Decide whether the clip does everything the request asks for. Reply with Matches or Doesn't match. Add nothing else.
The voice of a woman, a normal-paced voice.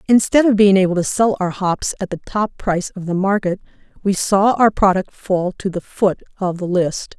Doesn't match